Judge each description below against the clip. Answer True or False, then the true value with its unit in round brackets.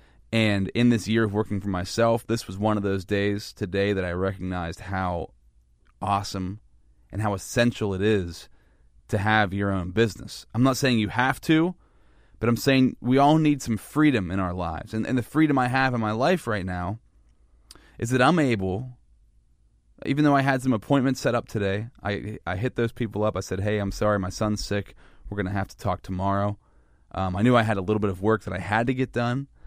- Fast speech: True (220 wpm)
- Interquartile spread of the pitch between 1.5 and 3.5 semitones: False (4.2 semitones)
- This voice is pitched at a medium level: False (105 Hz)